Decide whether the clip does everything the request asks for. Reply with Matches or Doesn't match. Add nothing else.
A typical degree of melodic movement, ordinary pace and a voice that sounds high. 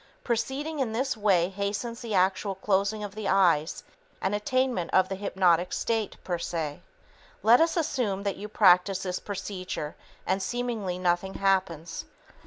Matches